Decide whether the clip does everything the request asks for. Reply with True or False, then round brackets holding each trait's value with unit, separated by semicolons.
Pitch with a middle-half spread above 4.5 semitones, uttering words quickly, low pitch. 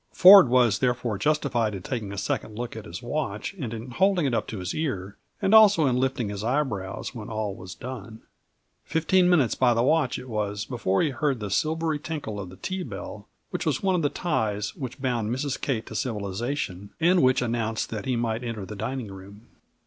True (5.4 semitones; 210 wpm; 120 Hz)